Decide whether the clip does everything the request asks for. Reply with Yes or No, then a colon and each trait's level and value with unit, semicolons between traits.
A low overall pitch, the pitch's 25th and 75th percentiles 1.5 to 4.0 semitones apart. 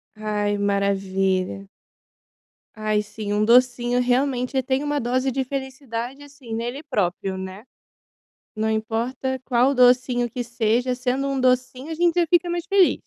No: high, 245 Hz; average, 3.7 semitones